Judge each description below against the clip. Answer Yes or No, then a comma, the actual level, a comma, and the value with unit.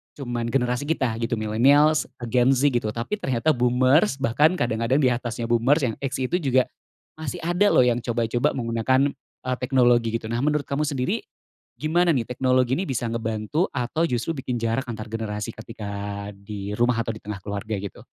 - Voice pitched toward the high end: No, low, 120 Hz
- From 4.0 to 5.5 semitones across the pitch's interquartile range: No, average, 3.2 semitones